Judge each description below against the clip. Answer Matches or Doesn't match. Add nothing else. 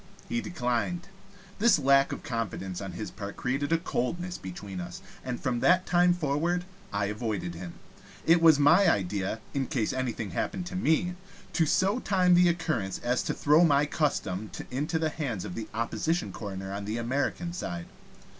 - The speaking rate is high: Doesn't match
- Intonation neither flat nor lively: Doesn't match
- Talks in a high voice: Doesn't match